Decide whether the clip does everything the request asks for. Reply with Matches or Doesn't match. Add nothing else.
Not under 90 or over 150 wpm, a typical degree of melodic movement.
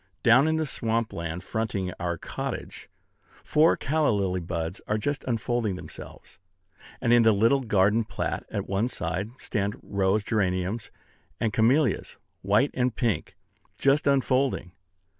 Matches